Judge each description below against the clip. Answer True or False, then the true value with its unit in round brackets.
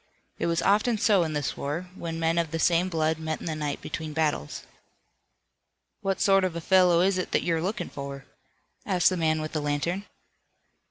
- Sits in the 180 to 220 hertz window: False (165 Hz)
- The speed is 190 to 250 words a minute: True (200 wpm)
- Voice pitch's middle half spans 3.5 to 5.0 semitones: False (2.9 semitones)